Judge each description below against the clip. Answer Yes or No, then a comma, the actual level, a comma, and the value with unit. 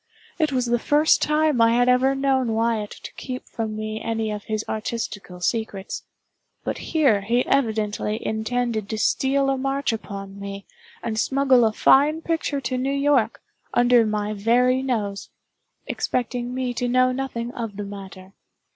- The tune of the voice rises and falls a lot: No, average, 3.4 semitones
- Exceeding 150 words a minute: Yes, average, 160 wpm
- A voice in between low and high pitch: No, high, 235 Hz